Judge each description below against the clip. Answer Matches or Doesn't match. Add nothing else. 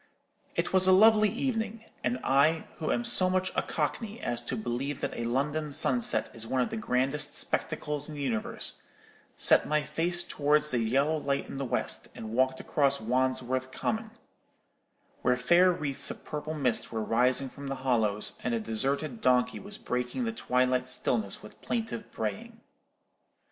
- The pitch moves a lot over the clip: Matches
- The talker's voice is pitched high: Doesn't match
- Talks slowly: Doesn't match